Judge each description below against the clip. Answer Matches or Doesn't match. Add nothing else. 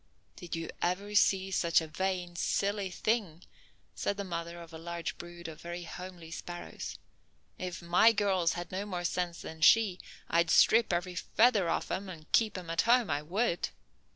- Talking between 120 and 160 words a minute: Doesn't match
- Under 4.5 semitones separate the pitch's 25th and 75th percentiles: Matches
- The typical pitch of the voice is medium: Matches